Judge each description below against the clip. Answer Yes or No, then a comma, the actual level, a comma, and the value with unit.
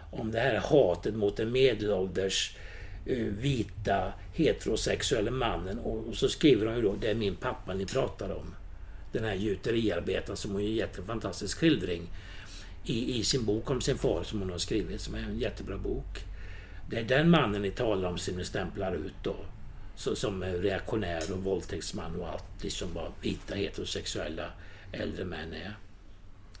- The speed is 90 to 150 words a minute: No, average, 170 wpm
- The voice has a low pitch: Yes, very low, 95 Hz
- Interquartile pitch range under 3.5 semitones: Yes, narrow, 2.4 semitones